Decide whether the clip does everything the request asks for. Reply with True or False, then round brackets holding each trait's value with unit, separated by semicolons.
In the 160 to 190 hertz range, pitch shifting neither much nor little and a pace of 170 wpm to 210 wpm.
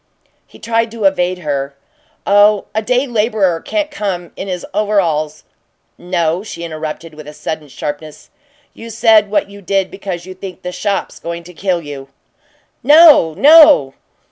False (185 Hz; 4.7 semitones; 160 wpm)